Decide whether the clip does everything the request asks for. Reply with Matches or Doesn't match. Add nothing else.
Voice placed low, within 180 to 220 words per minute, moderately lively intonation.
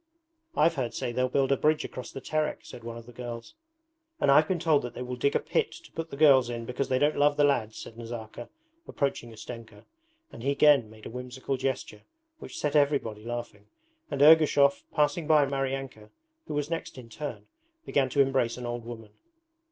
Matches